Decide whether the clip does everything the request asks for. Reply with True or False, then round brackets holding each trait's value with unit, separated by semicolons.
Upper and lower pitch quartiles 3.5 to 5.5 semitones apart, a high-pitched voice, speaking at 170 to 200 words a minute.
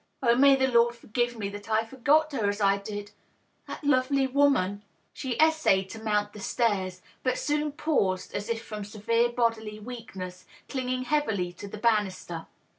True (4.1 semitones; 225 Hz; 180 wpm)